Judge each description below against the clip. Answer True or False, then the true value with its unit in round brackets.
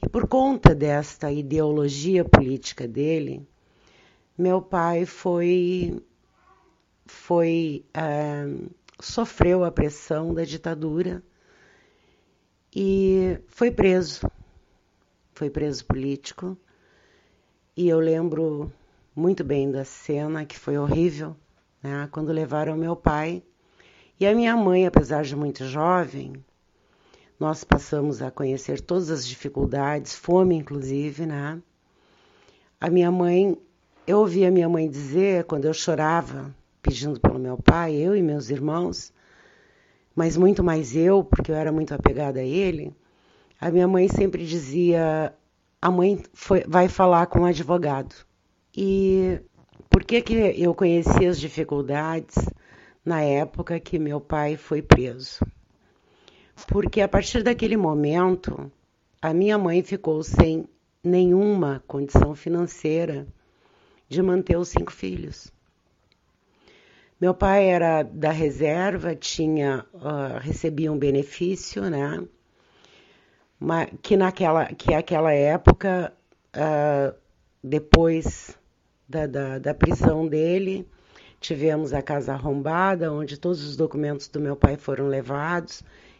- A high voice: False (160 Hz)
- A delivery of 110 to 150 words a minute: True (120 wpm)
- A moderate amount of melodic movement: True (3.7 semitones)